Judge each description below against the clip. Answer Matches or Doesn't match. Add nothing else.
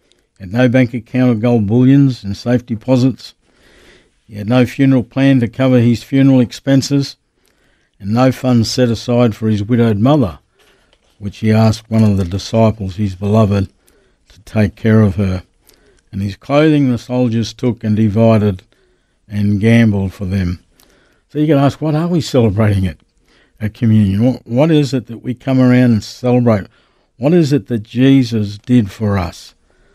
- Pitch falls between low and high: Doesn't match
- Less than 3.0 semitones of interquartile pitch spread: Doesn't match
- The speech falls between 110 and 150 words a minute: Doesn't match